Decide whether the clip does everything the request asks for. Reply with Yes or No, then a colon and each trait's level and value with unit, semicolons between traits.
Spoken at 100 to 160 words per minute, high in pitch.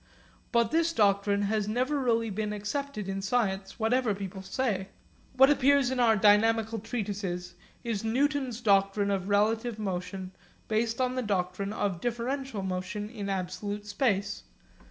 Yes: average, 140 wpm; high, 210 Hz